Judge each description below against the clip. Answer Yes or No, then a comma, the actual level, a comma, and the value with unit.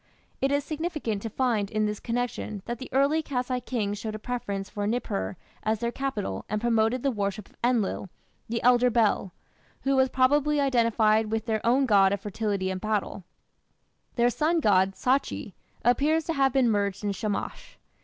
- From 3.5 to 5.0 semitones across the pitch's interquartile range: Yes, average, 4.0 semitones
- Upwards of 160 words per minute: Yes, average, 175 wpm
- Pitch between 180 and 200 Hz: No, high, 230 Hz